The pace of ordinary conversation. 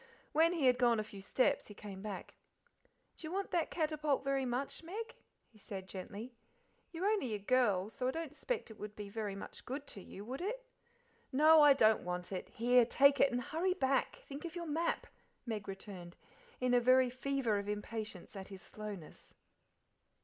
Yes: average, 190 wpm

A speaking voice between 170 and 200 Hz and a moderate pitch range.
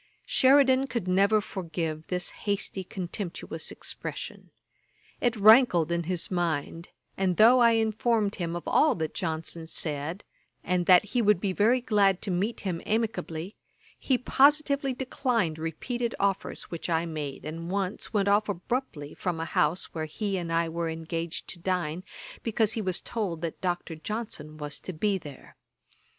Yes: medium, 185 Hz; average, 4.7 semitones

